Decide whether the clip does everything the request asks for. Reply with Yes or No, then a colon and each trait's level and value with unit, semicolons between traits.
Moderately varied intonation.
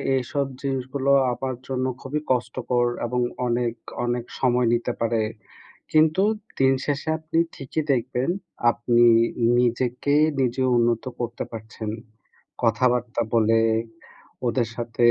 No: narrow, 2.0 semitones